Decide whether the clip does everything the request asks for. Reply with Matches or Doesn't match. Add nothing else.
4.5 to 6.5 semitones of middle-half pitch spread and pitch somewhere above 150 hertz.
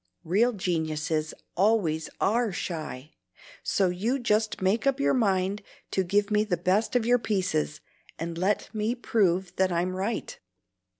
Doesn't match